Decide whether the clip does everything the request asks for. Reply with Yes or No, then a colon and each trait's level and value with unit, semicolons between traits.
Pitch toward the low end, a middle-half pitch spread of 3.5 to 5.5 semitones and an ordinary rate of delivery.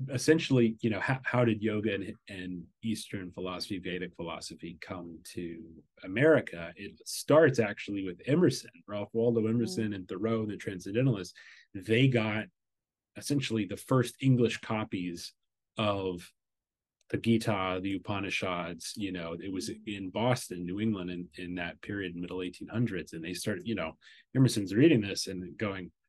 Yes: low, 100 Hz; average, 3.9 semitones; average, 150 wpm